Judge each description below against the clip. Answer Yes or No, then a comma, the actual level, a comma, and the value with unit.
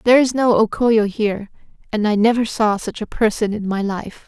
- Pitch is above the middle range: Yes, high, 215 Hz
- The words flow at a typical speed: No, fast, 225 wpm